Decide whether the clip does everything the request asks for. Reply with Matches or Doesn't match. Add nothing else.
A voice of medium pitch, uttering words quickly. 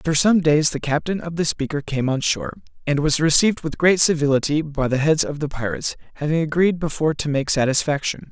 Matches